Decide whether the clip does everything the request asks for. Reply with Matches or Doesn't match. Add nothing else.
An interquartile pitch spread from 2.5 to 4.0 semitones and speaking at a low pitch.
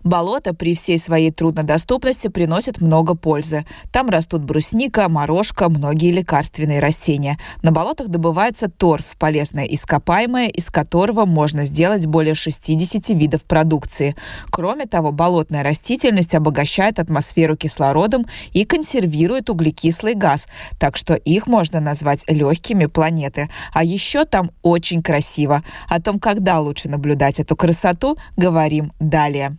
Doesn't match